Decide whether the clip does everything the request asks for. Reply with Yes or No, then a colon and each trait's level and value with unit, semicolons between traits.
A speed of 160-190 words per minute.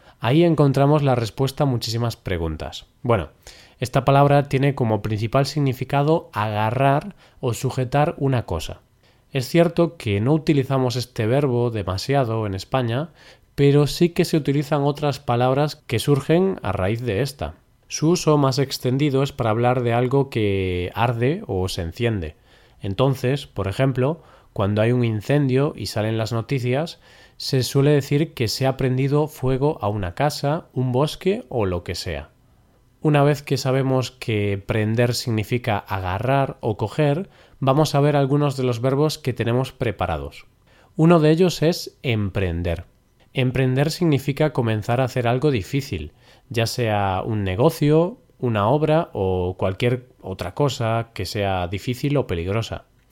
No: average, 150 wpm